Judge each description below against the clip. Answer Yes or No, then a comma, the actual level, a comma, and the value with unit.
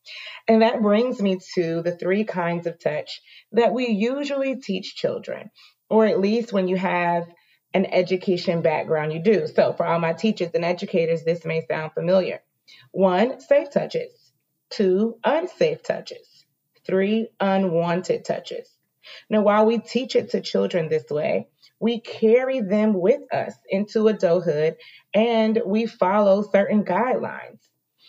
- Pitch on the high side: Yes, high, 205 Hz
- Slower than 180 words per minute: Yes, average, 145 wpm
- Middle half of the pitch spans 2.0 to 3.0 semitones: No, average, 4.8 semitones